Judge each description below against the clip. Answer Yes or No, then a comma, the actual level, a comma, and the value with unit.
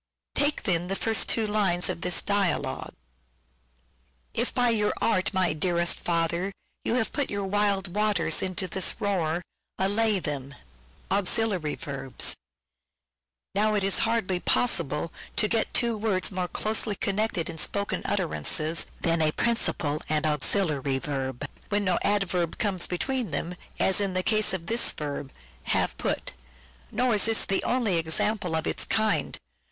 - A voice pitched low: No, medium, 185 Hz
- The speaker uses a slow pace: No, average, 155 wpm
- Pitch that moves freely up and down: No, average, 4.8 semitones